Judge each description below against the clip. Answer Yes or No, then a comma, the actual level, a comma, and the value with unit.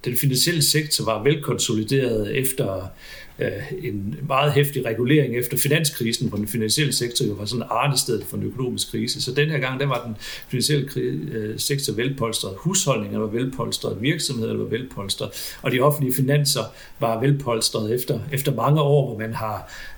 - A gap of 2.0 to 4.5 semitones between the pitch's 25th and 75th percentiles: Yes, average, 3.9 semitones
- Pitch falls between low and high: No, low, 130 Hz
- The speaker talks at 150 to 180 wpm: Yes, average, 160 wpm